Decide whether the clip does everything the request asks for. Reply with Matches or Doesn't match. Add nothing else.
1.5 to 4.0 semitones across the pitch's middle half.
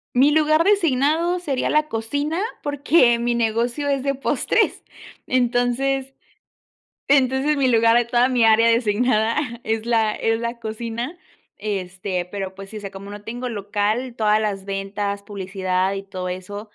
Doesn't match